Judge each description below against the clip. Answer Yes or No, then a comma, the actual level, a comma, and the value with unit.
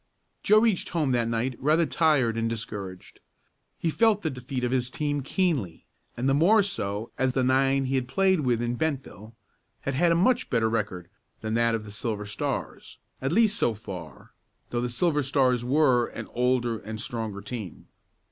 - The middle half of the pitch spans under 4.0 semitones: No, average, 4.9 semitones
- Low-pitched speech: Yes, low, 125 Hz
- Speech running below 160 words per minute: No, average, 185 wpm